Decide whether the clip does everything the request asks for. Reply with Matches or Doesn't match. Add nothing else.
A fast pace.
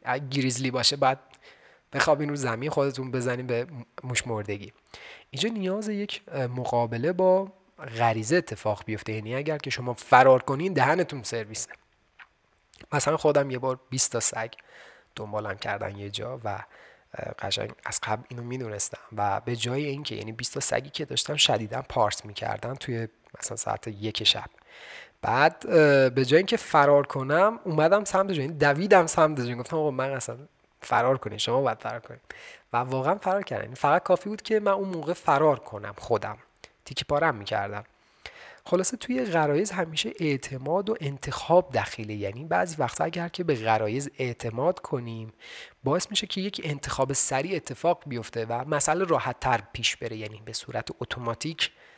Matches